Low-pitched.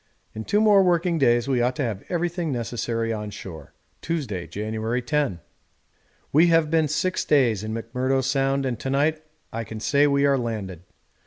Yes: low, 130 Hz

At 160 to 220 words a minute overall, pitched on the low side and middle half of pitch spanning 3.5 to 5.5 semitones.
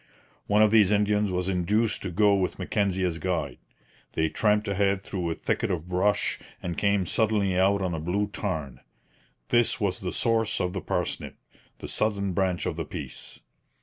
No: average, 180 wpm; very low, 95 Hz; narrow, 2.5 semitones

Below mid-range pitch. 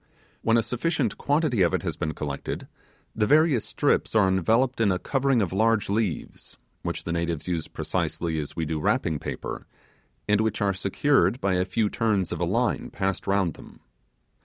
Yes: low, 100 Hz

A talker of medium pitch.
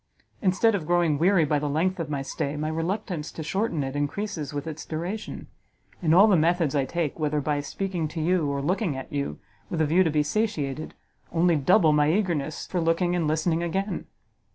Yes: medium, 160 Hz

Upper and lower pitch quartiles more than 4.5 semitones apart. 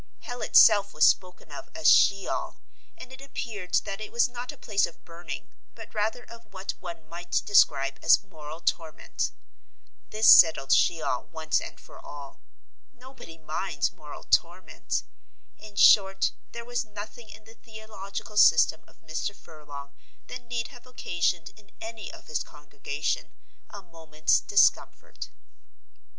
Yes: wide, 5.6 semitones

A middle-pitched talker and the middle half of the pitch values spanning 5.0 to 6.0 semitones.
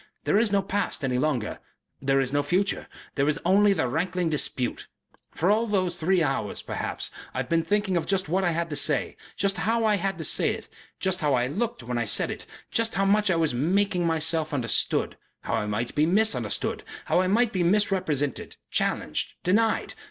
Yes: medium, 175 Hz; wide, 5.4 semitones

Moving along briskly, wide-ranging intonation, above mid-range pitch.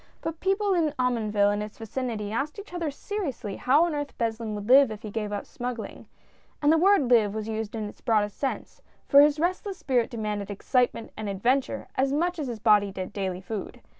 Yes: fast, 230 wpm; wide, 5.7 semitones; high, 235 Hz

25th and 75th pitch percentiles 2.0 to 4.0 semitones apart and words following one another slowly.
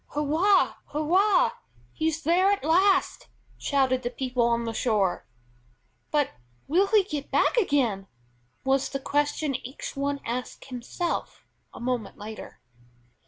No: average, 5.2 semitones; slow, 125 wpm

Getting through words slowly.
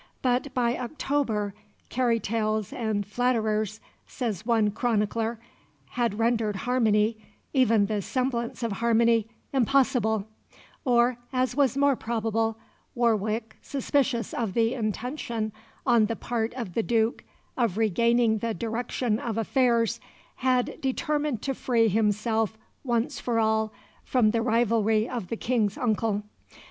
Yes: slow, 125 wpm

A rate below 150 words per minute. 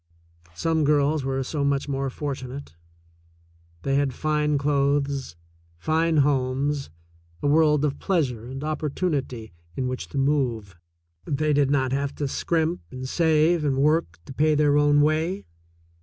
Yes: average, 140 wpm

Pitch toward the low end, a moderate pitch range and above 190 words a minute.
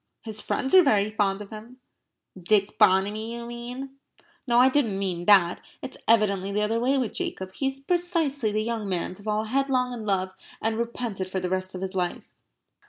No: high, 215 Hz; average, 4.2 semitones; average, 200 wpm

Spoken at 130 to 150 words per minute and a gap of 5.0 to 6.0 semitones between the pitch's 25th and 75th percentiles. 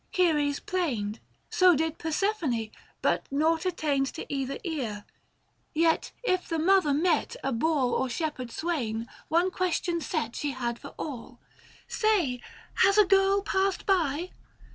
Yes: average, 140 wpm; wide, 5.6 semitones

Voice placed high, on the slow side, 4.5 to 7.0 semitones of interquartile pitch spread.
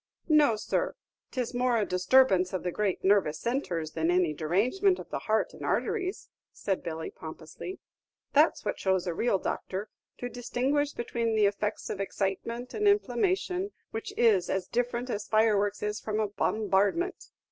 No: high, 215 Hz; average, 160 wpm; average, 4.9 semitones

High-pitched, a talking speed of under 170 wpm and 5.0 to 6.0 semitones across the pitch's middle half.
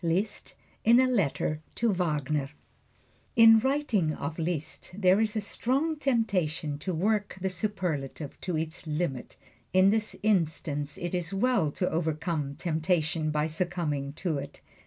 No: medium, 175 Hz; average, 150 wpm; average, 5.3 semitones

